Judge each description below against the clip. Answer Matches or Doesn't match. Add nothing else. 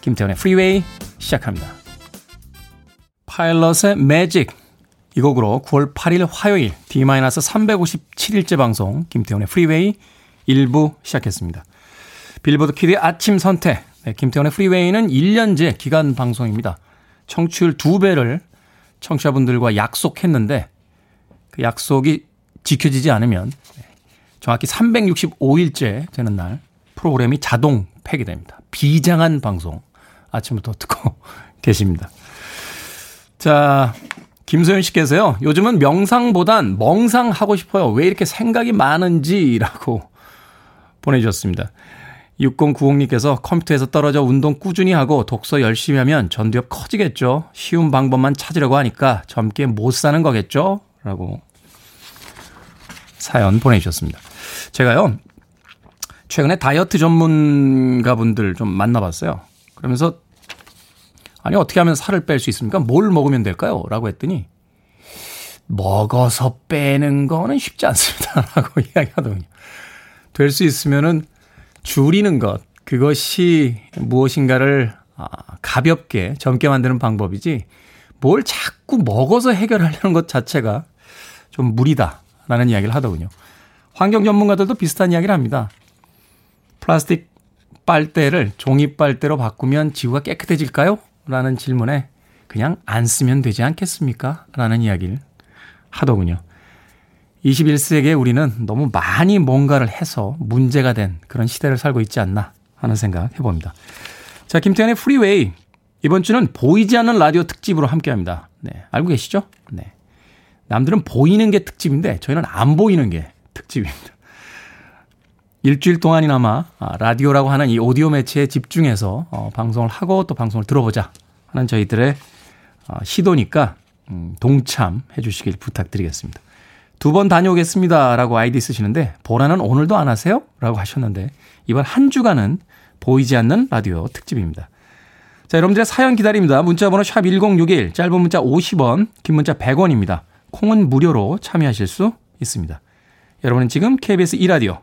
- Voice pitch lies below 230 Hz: Matches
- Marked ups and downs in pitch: Matches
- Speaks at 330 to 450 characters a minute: Doesn't match